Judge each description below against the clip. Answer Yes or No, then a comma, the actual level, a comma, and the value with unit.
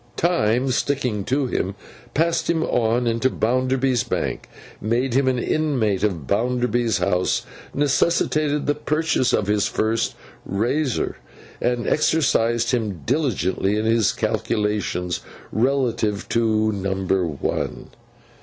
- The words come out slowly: Yes, slow, 115 wpm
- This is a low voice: Yes, low, 120 Hz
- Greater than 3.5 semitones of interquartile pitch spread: Yes, average, 4.3 semitones